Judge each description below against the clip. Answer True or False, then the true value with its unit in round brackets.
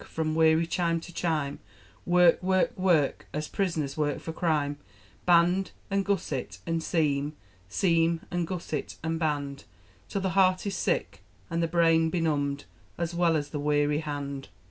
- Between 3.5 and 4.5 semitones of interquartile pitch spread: False (3.0 semitones)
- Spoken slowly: False (155 wpm)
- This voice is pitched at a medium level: True (165 Hz)